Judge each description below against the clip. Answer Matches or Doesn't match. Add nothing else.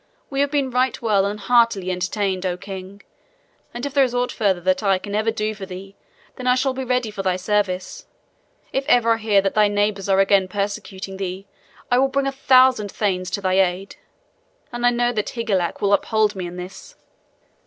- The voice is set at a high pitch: Matches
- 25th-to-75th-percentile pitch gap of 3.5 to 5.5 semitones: Matches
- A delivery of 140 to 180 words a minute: Doesn't match